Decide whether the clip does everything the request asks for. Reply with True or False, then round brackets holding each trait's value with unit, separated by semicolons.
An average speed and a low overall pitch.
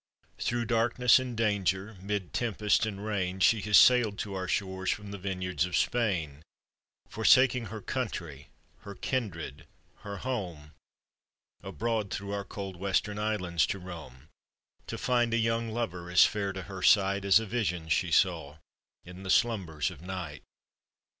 True (155 wpm; 100 Hz)